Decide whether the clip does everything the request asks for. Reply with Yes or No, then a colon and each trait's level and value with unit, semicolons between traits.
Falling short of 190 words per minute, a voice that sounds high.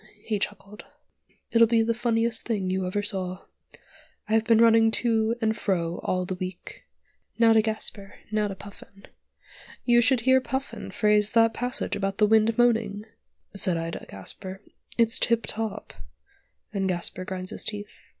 Yes: average, 155 wpm; high, 215 Hz